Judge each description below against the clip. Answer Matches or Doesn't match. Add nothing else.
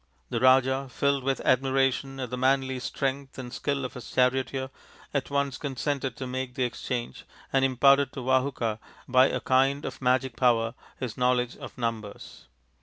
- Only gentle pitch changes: Matches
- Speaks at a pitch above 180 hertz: Doesn't match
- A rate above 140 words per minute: Matches